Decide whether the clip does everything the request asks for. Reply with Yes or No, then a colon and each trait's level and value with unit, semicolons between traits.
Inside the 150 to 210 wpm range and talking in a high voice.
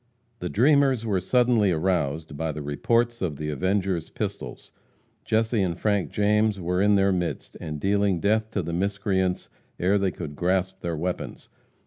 No: average, 160 wpm; very low, 95 Hz